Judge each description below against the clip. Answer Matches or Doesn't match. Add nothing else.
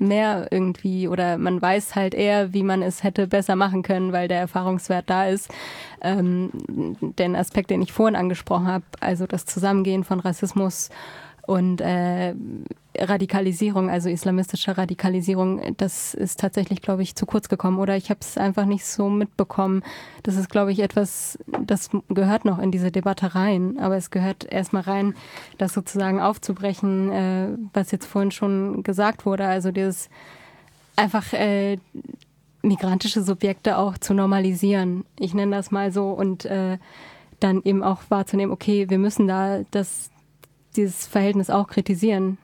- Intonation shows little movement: Matches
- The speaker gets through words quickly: Doesn't match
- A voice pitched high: Matches